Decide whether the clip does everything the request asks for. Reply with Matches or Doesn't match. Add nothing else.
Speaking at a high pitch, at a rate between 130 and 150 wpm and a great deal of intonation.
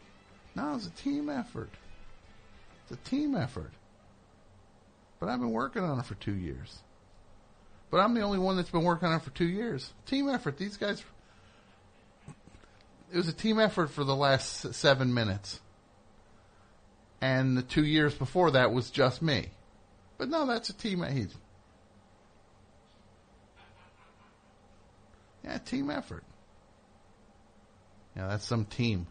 Doesn't match